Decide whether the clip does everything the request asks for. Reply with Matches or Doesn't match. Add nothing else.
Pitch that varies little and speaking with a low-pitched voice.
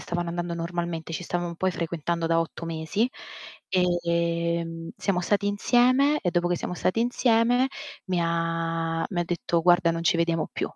Doesn't match